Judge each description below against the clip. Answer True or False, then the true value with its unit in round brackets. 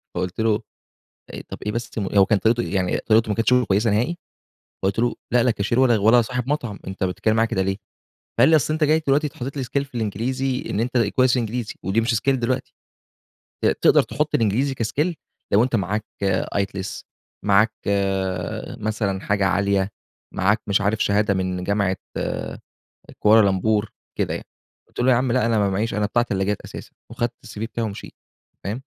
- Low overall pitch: True (110 Hz)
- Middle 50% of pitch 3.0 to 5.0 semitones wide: True (3.6 semitones)